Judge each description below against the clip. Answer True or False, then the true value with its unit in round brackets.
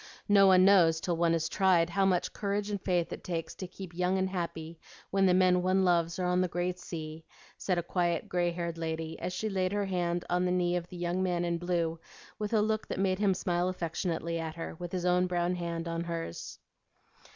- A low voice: False (180 Hz)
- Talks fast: True (230 wpm)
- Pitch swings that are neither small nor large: False (1.7 semitones)